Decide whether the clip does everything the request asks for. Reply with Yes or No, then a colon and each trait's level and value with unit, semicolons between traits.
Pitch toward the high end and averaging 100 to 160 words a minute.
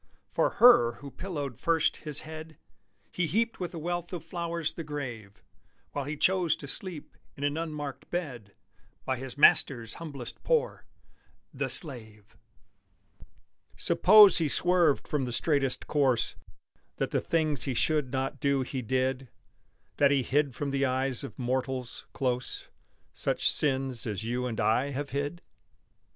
No: medium, 140 Hz; average, 150 wpm